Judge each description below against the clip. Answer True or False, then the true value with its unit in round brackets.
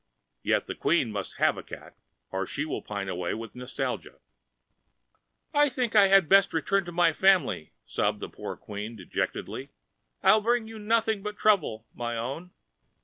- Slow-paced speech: False (170 wpm)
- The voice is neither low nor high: True (170 Hz)